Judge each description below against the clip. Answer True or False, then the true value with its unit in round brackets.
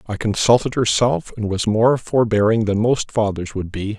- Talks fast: False (180 wpm)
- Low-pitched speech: True (110 Hz)